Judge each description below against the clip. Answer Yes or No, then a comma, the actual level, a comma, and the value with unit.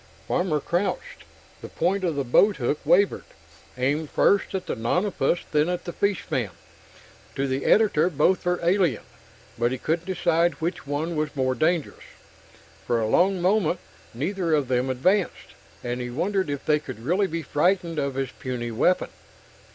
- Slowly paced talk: No, average, 160 wpm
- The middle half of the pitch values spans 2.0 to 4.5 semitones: No, average, 5.3 semitones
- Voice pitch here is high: No, medium, 160 Hz